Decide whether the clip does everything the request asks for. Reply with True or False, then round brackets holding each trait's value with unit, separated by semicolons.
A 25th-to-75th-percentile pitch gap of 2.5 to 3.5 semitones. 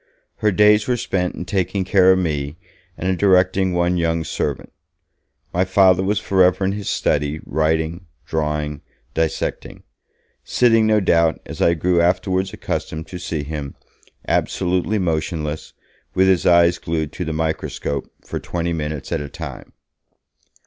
True (3.0 semitones)